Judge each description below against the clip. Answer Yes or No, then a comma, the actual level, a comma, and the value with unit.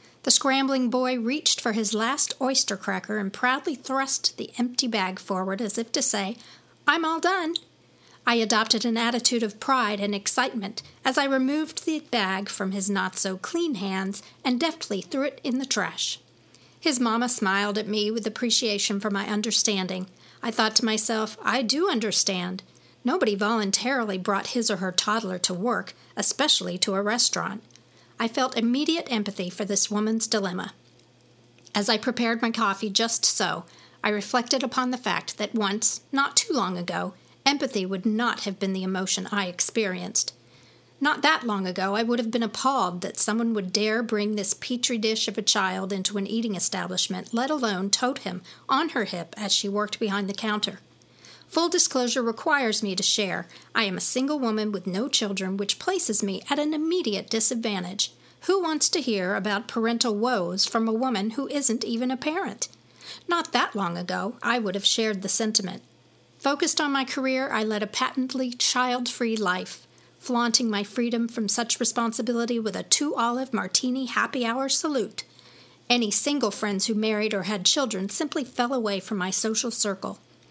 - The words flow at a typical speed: Yes, average, 175 wpm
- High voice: Yes, high, 225 Hz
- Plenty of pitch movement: No, average, 4.1 semitones